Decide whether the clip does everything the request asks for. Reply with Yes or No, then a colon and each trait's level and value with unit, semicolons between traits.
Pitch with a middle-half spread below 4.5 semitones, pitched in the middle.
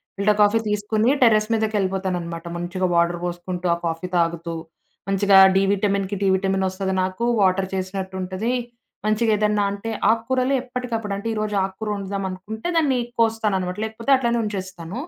No: average, 2.8 semitones; high, 200 Hz